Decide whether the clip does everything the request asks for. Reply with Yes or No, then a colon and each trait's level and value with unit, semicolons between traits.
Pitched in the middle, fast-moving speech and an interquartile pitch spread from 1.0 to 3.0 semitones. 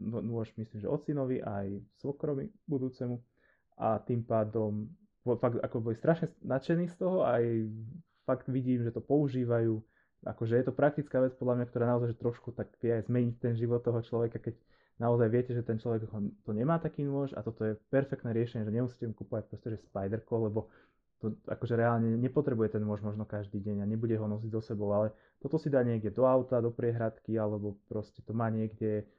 No: low, 115 Hz; fast, 195 wpm; average, 2.7 semitones